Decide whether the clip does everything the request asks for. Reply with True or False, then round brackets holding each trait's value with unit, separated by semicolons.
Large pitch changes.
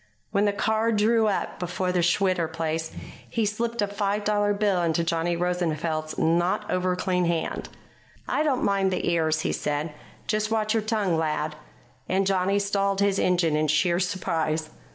False (3.8 semitones)